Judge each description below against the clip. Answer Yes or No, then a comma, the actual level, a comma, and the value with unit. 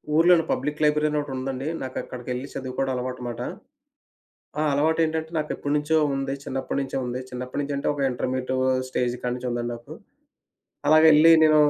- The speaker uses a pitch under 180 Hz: Yes, low, 135 Hz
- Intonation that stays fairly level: No, average, 3.0 semitones